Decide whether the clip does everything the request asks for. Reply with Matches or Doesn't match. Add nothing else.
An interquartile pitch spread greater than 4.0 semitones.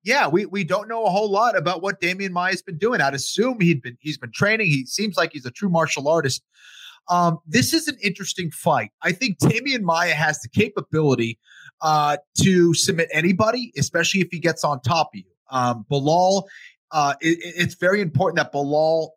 Matches